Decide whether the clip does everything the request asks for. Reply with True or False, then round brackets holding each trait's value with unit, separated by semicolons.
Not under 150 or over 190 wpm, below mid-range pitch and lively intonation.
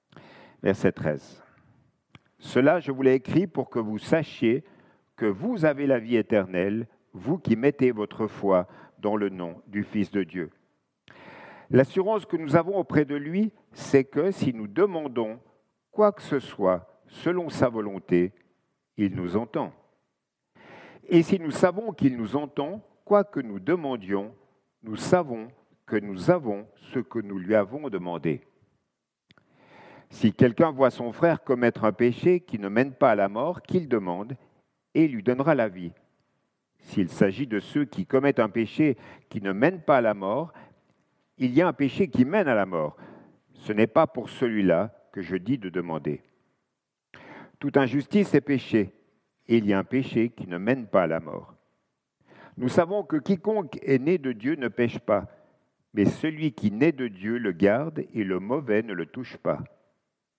True (170 wpm; 130 Hz; 6.8 semitones)